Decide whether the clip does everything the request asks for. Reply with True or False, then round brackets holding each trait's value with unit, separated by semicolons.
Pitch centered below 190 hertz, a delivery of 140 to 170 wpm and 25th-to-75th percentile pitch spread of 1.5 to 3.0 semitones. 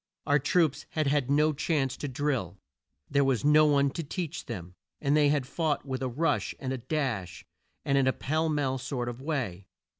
False (140 Hz; 200 wpm; 2.6 semitones)